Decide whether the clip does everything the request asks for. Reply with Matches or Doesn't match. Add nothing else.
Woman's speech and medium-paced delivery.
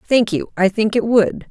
Doesn't match